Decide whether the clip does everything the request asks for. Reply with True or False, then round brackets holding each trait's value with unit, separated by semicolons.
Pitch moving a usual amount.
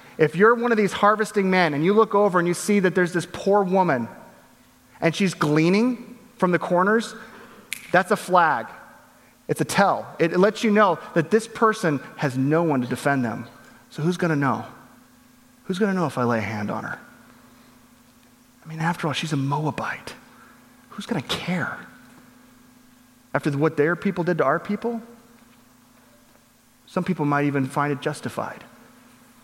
False (6.2 semitones)